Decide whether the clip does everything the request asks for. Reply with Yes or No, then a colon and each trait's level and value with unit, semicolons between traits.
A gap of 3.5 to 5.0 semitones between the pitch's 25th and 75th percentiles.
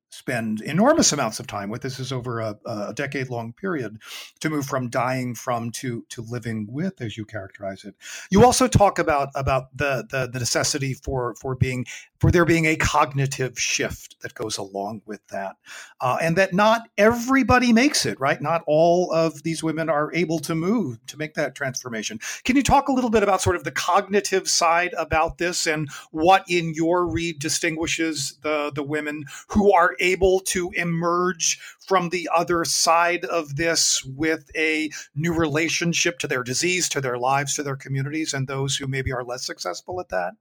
Yes: average, 4.7 semitones